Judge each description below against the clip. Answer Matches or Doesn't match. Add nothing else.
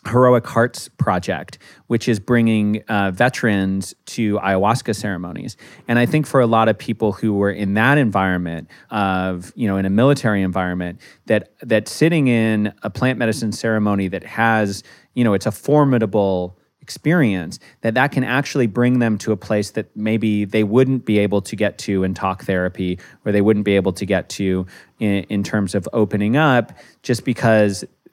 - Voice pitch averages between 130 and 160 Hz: Doesn't match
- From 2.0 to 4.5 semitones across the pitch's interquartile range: Matches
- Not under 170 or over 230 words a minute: Matches